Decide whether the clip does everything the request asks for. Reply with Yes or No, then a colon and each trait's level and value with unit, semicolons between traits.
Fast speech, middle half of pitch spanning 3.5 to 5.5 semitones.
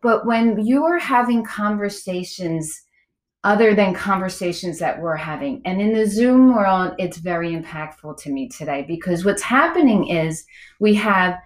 No: average, 150 wpm; average, 4.5 semitones